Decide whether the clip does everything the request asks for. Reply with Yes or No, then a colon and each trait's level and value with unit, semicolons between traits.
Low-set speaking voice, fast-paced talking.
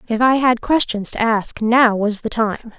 No: high, 230 Hz; fast, 215 wpm